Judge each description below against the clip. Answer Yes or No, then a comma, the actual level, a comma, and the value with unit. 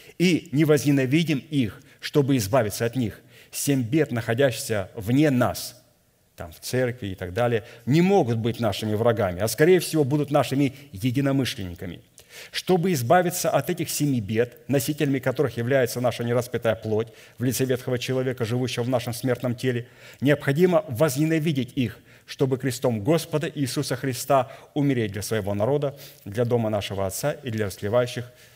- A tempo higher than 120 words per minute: Yes, average, 145 wpm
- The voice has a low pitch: Yes, low, 130 Hz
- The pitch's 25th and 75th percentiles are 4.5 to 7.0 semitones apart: No, average, 3.8 semitones